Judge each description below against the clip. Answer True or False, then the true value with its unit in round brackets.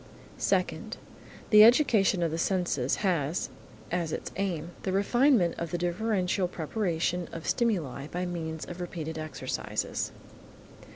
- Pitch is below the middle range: False (175 Hz)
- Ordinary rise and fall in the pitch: True (3.3 semitones)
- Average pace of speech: False (125 wpm)